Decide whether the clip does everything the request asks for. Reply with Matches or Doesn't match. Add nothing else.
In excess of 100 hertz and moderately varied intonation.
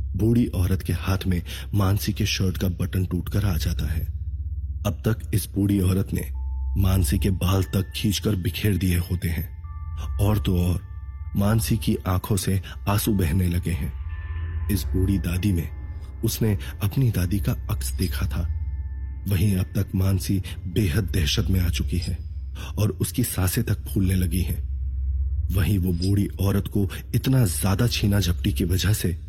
Doesn't match